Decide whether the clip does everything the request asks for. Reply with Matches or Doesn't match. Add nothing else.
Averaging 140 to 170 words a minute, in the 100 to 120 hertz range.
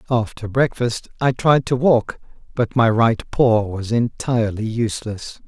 Matches